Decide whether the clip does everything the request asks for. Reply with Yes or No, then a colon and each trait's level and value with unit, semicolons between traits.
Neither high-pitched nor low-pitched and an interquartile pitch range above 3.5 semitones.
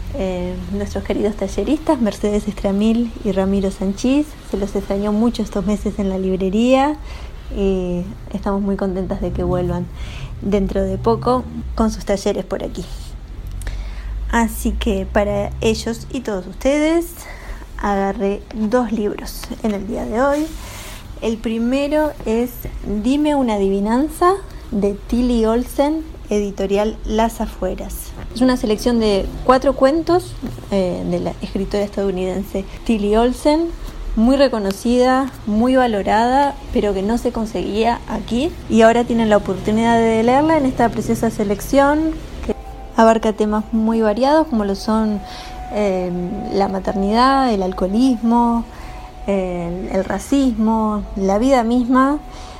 No: high, 215 Hz; average, 3.9 semitones